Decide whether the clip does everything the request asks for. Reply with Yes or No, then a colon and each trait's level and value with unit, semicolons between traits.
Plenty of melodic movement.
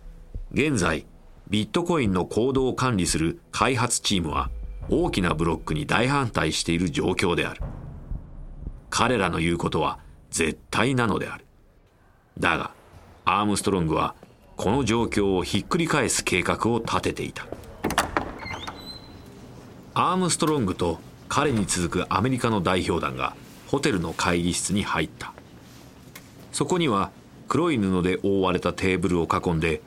No: average, 4.3 semitones